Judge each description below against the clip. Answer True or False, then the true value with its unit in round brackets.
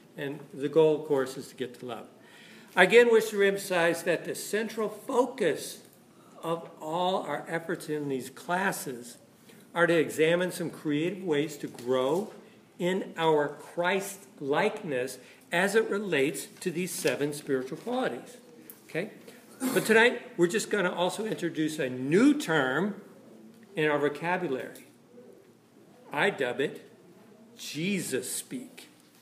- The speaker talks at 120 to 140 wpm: True (135 wpm)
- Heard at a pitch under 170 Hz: False (175 Hz)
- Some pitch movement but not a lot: False (5.7 semitones)